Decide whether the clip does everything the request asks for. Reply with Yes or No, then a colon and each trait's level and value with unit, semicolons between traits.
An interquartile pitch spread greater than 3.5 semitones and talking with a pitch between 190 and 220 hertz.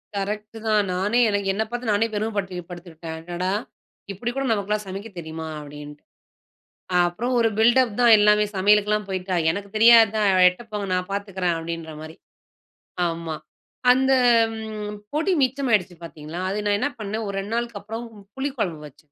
Yes: average, 4.2 semitones; high, 205 Hz